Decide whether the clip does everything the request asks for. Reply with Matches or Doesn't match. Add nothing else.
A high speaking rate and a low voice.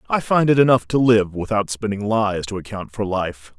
Matches